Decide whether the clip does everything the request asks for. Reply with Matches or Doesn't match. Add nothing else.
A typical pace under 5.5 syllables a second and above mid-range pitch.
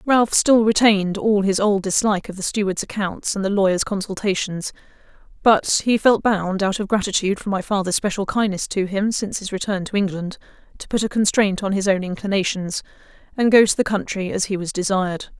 Doesn't match